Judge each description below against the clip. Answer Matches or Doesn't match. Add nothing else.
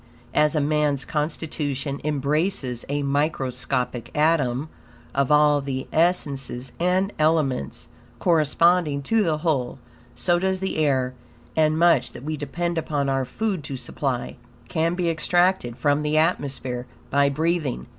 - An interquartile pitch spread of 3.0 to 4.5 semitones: Matches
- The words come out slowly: Matches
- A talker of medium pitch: Matches